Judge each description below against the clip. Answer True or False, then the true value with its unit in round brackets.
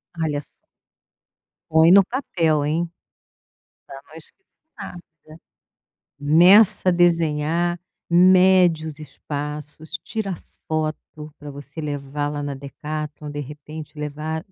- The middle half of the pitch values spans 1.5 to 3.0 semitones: True (2.7 semitones)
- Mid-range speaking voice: True (155 Hz)